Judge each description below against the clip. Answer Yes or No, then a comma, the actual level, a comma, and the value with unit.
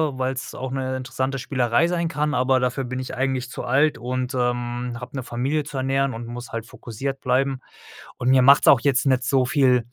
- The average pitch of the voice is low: Yes, low, 130 Hz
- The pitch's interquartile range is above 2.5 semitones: No, narrow, 1.5 semitones